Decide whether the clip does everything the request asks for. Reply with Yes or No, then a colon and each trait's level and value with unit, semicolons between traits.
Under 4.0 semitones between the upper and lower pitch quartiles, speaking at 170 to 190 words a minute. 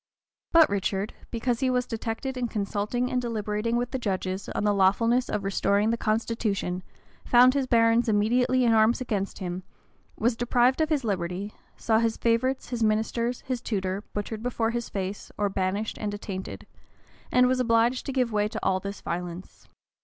Yes: average, 3.3 semitones; average, 175 wpm